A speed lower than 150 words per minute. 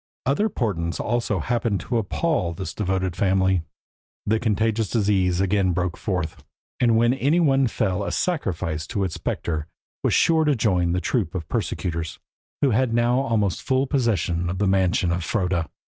No: average, 170 wpm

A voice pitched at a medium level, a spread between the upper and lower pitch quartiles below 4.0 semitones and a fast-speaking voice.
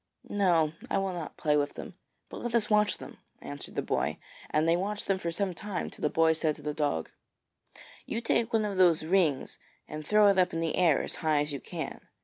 No: medium, 170 Hz; average, 4.7 semitones; fast, 230 wpm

